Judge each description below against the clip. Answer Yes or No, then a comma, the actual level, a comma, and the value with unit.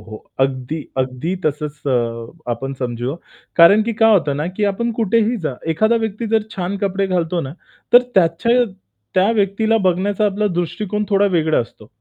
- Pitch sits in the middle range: Yes, medium, 180 Hz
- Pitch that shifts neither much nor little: No, wide, 7.0 semitones